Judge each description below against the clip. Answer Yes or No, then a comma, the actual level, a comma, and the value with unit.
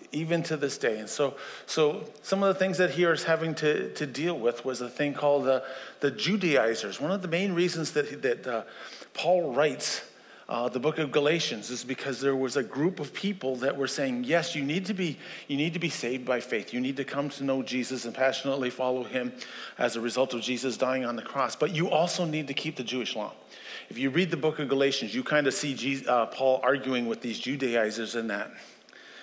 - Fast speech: Yes, fast, 230 wpm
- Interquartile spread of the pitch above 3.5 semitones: Yes, average, 4.1 semitones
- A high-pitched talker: No, medium, 140 Hz